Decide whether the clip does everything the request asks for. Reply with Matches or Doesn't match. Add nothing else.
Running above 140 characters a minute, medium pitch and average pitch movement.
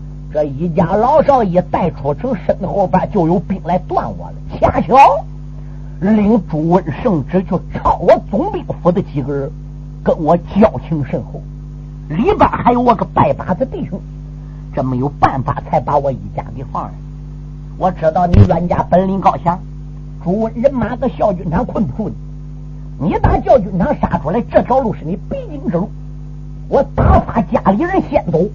Matches